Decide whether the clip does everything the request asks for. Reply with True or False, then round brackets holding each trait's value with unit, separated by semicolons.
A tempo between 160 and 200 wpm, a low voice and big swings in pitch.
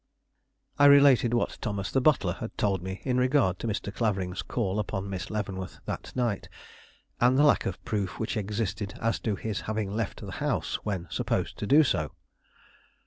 False (180 wpm; 105 Hz; 3.9 semitones)